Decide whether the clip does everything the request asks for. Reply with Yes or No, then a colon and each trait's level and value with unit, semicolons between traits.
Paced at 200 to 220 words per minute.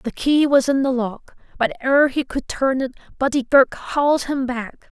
Yes: fast, 205 wpm